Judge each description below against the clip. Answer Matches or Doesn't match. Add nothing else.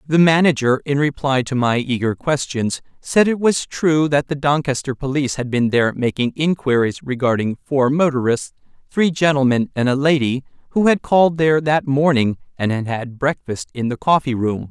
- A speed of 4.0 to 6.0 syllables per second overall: Matches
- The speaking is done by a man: Matches